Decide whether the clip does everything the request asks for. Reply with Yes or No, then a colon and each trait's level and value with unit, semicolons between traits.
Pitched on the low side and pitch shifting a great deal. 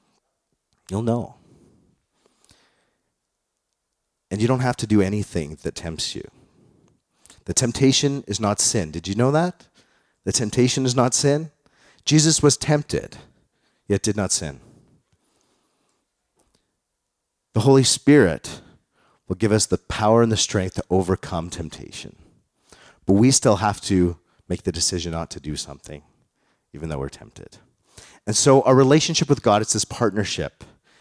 Yes: low, 105 Hz; wide, 6.1 semitones